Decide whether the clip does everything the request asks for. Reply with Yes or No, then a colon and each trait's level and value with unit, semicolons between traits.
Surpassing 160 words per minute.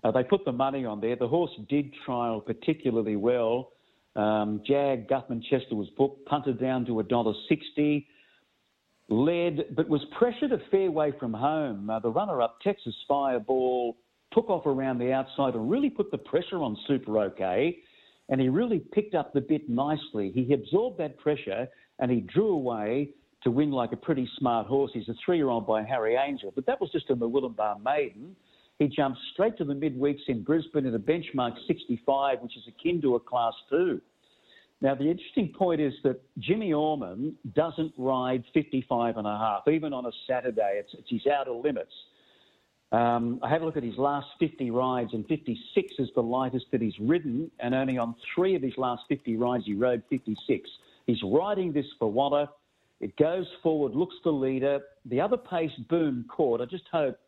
Yes: average, 190 wpm